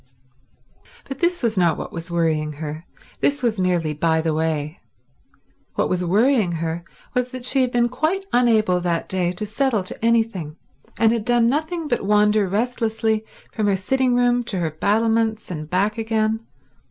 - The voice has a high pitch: Yes, high, 215 Hz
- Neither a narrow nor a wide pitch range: No, wide, 5.8 semitones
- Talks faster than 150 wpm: Yes, average, 170 wpm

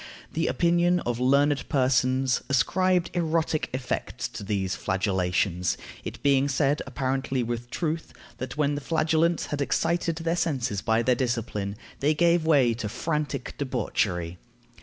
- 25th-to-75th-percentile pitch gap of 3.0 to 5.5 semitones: Yes, average, 5.2 semitones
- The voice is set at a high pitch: No, low, 135 Hz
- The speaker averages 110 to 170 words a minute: Yes, average, 140 wpm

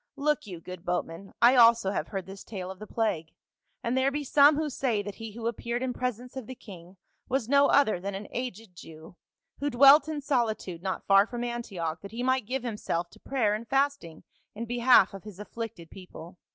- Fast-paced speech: Yes, fast, 215 wpm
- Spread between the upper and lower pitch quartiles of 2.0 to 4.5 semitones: No, average, 5.1 semitones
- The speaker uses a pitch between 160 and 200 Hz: No, high, 225 Hz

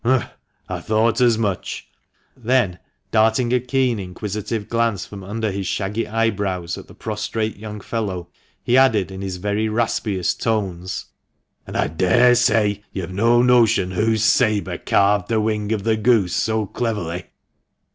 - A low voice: Yes, low, 110 Hz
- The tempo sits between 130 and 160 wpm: Yes, average, 155 wpm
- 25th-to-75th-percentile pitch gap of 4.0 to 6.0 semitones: No, average, 2.8 semitones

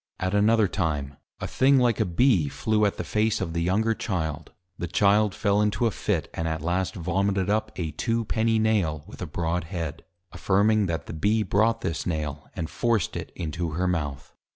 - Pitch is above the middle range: No, very low, 95 Hz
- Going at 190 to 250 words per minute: Yes, average, 200 wpm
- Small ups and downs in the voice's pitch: No, average, 4.8 semitones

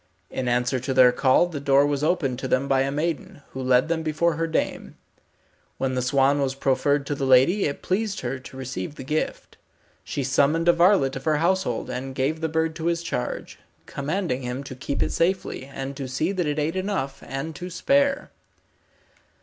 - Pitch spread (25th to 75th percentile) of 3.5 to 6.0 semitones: Yes, average, 3.9 semitones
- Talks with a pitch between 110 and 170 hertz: Yes, medium, 140 Hz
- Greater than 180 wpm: Yes, average, 200 wpm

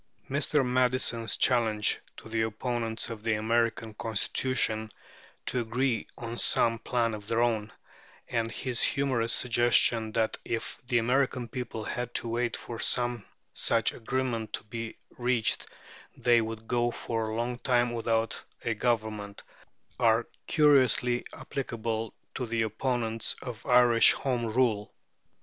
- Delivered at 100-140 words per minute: Yes, slow, 135 wpm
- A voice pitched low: Yes, low, 115 Hz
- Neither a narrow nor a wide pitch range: No, narrow, 1.7 semitones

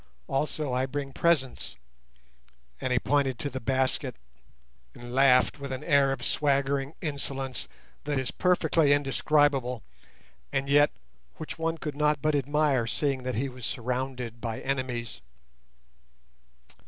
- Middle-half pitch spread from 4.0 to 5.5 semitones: No, narrow, 2.4 semitones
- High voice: No, low, 135 Hz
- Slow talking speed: Yes, slow, 130 wpm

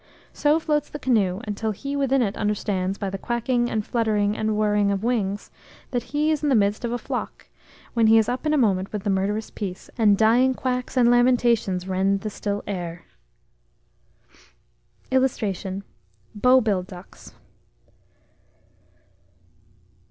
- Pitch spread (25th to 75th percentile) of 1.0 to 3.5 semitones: No, average, 3.9 semitones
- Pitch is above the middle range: Yes, high, 215 Hz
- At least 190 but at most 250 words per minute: No, average, 150 wpm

